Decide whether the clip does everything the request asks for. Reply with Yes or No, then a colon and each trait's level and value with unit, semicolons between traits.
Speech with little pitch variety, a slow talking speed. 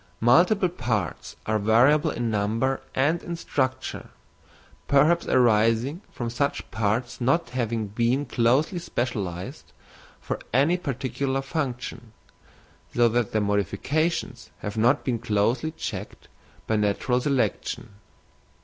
No: average, 4.2 semitones; slow, 115 wpm